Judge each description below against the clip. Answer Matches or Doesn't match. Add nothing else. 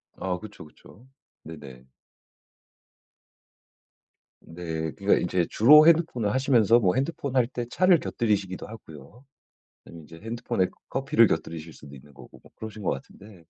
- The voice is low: Matches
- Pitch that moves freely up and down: Matches